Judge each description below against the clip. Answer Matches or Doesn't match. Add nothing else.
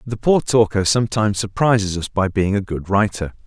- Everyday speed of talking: Matches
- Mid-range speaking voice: Doesn't match